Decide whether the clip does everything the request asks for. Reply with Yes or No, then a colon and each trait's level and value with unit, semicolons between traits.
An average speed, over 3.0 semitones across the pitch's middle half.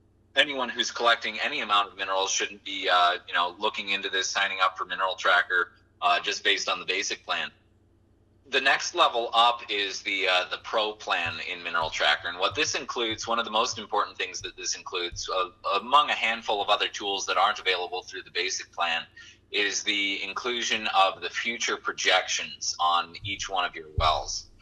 No: average, 195 wpm; average, 2.7 semitones